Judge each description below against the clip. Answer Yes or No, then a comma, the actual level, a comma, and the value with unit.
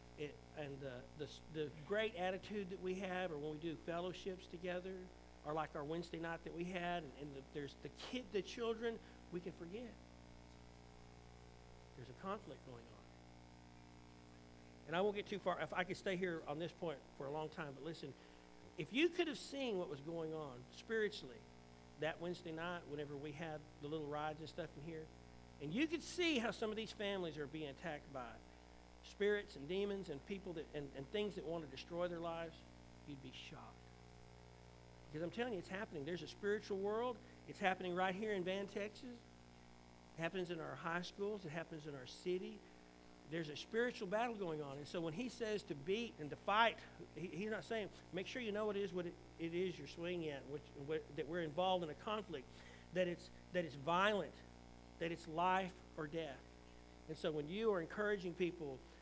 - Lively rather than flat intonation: Yes, wide, 7.1 semitones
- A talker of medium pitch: Yes, medium, 165 Hz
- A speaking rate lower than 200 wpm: No, fast, 205 wpm